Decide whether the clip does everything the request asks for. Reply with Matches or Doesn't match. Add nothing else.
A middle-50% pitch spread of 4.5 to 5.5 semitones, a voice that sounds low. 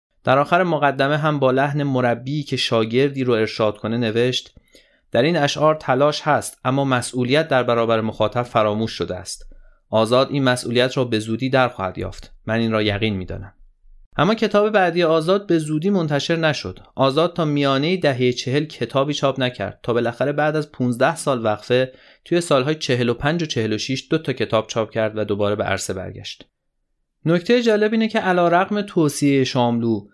Matches